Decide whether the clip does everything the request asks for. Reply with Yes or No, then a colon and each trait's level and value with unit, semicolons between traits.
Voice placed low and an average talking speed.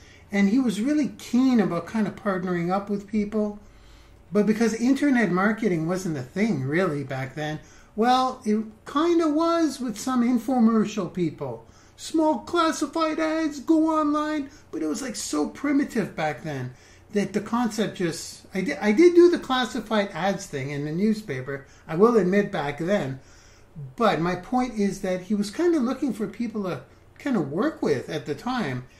No: high, 210 Hz; average, 175 wpm